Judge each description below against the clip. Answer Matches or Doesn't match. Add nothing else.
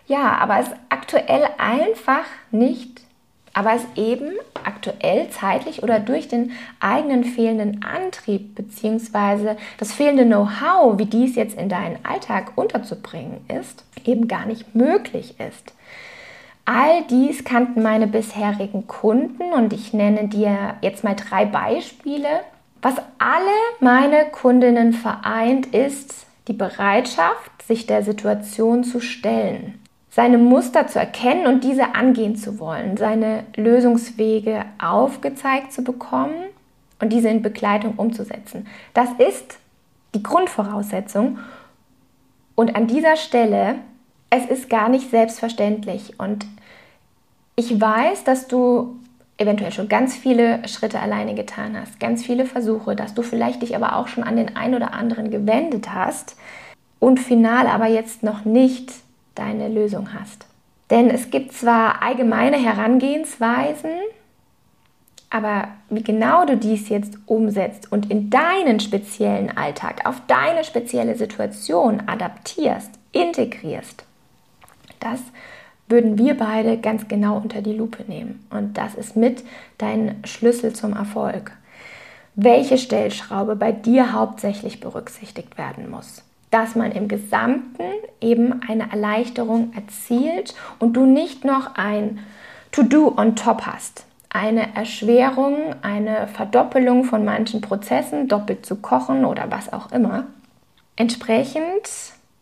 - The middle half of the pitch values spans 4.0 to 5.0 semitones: Doesn't match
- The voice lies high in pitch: Matches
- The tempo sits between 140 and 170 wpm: Doesn't match